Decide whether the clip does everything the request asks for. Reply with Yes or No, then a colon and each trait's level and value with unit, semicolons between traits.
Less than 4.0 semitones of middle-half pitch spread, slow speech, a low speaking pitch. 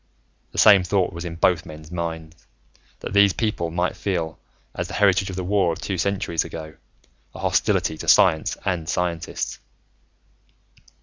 No: average, 2.9 semitones; average, 160 wpm; very low, 90 Hz